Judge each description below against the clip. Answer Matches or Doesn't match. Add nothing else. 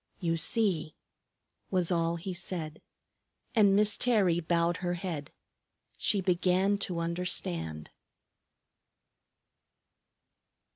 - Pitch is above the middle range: Doesn't match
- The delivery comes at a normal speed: Doesn't match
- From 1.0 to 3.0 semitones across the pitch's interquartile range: Matches